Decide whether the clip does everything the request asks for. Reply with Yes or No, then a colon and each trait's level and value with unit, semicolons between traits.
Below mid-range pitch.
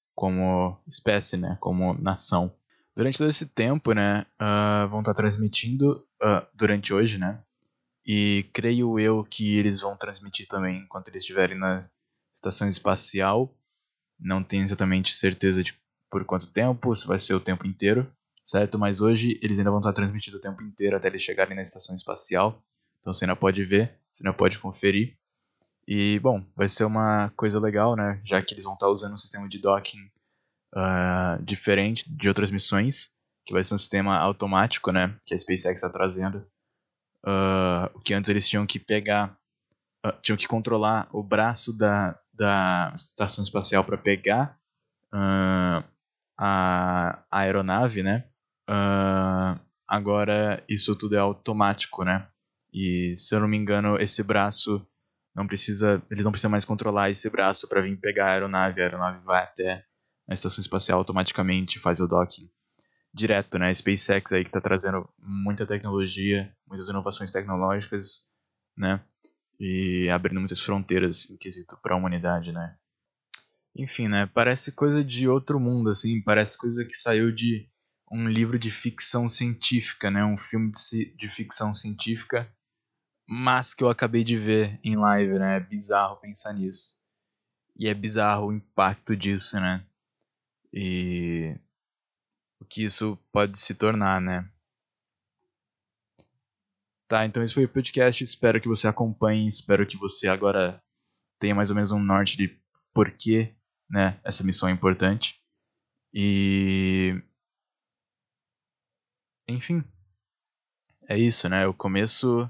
Yes: low, 100 Hz